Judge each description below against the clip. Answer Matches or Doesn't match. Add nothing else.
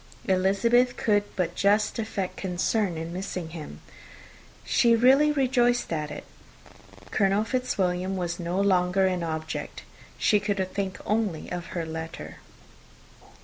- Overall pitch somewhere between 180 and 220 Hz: Matches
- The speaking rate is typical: Doesn't match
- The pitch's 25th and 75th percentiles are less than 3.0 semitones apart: Doesn't match